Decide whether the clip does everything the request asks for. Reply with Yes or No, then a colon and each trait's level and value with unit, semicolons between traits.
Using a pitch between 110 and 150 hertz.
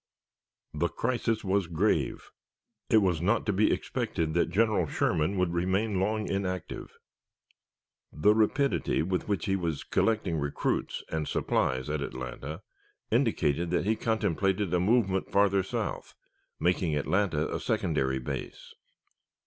No: very low, 90 Hz